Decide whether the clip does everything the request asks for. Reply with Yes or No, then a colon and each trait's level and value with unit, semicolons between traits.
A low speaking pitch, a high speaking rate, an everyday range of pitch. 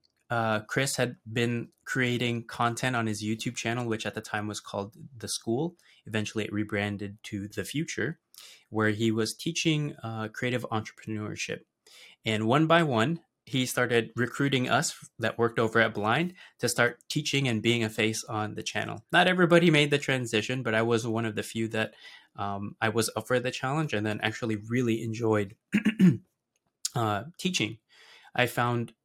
No: low, 115 Hz; average, 170 wpm; average, 3.1 semitones